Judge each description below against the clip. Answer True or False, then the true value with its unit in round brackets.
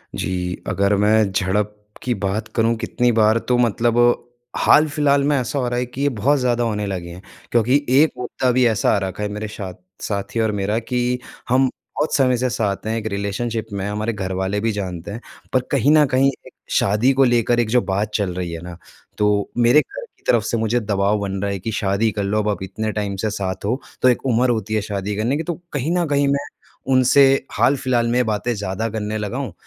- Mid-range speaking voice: False (110 Hz)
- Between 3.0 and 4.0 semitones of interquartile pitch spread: True (3.6 semitones)